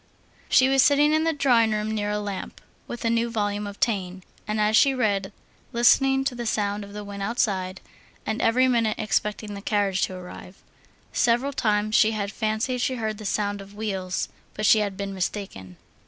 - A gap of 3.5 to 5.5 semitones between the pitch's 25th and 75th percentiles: No, average, 2.7 semitones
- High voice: Yes, high, 215 Hz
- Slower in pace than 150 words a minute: No, average, 195 wpm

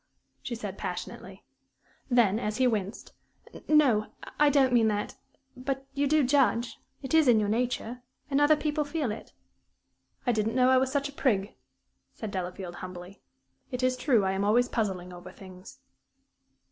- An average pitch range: Yes, average, 4.7 semitones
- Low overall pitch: No, high, 240 Hz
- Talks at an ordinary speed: Yes, average, 165 wpm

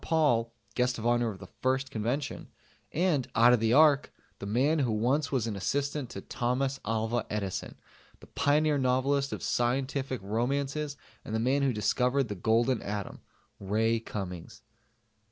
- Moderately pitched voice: No, low, 125 Hz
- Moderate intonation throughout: Yes, average, 3.8 semitones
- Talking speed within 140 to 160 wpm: Yes, average, 155 wpm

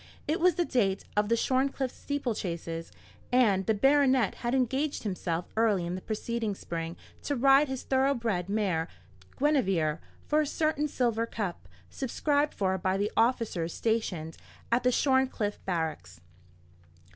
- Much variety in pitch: Yes, wide, 6.1 semitones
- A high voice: Yes, high, 230 Hz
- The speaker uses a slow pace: No, average, 145 wpm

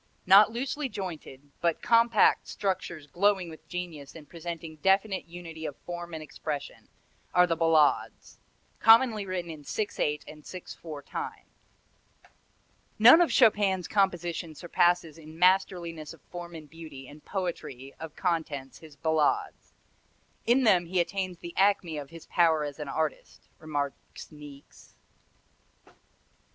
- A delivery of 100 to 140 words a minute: Yes, slow, 135 wpm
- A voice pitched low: No, medium, 170 Hz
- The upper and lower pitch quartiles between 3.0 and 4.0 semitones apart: Yes, average, 3.5 semitones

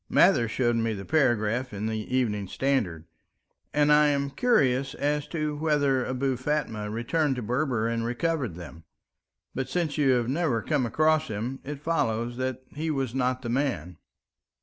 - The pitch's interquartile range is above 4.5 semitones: No, average, 4.2 semitones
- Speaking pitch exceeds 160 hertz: No, low, 130 Hz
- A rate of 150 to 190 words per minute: Yes, average, 165 wpm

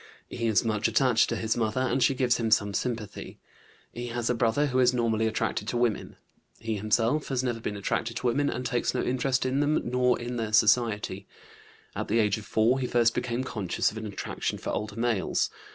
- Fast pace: Yes, fast, 215 wpm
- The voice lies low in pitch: Yes, low, 115 Hz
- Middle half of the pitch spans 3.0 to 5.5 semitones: No, narrow, 2.4 semitones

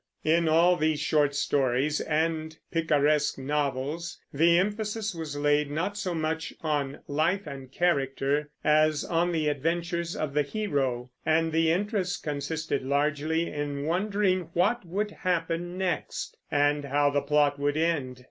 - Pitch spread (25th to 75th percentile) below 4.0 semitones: Yes, average, 2.9 semitones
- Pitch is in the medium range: Yes, medium, 155 Hz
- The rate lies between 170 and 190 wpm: No, average, 140 wpm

